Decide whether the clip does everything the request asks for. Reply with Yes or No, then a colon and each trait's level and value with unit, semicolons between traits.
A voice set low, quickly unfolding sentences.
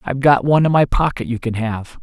Yes: low, 130 Hz; fast, 265 wpm